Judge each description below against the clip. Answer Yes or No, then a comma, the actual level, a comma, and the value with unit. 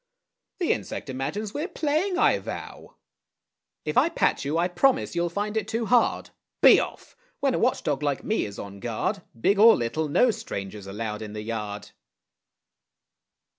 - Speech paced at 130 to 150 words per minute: No, average, 170 wpm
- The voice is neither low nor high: Yes, medium, 170 Hz